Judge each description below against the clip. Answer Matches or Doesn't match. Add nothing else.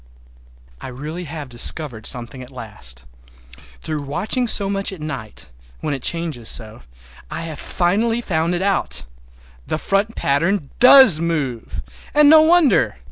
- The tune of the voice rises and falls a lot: Matches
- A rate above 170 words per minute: Doesn't match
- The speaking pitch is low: Doesn't match